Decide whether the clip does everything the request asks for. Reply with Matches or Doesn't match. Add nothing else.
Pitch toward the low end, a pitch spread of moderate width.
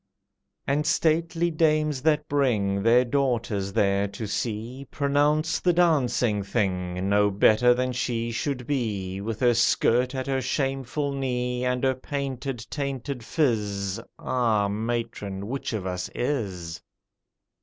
Matches